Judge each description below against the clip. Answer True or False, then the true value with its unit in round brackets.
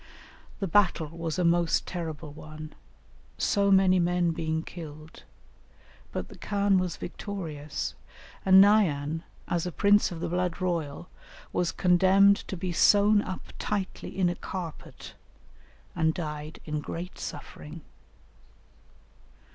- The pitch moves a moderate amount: True (3.2 semitones)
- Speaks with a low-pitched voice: False (175 Hz)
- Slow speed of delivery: True (125 wpm)